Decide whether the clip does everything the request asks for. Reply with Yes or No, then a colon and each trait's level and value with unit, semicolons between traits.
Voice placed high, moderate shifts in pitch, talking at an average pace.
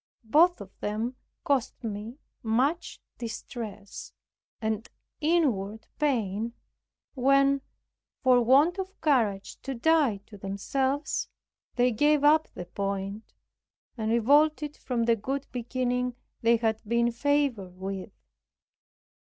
No: high, 240 Hz; average, 4.6 semitones; slow, 110 wpm